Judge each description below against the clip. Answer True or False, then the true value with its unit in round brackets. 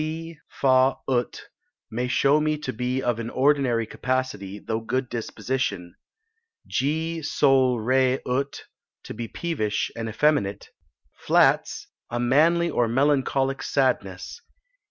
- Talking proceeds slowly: True (120 wpm)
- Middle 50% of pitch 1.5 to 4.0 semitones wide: True (3.6 semitones)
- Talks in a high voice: False (130 Hz)